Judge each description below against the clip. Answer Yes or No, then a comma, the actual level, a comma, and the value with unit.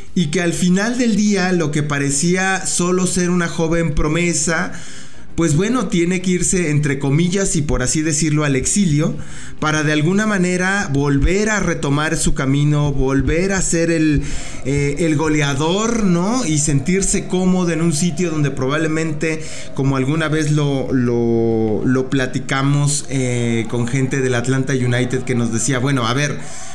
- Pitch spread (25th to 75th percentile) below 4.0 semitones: No, average, 4.5 semitones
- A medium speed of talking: Yes, average, 160 wpm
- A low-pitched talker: No, medium, 155 Hz